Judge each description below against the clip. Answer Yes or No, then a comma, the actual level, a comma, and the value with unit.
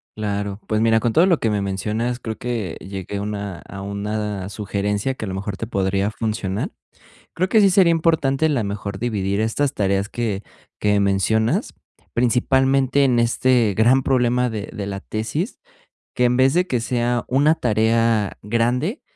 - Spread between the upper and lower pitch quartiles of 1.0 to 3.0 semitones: No, average, 4.1 semitones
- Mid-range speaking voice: No, low, 110 Hz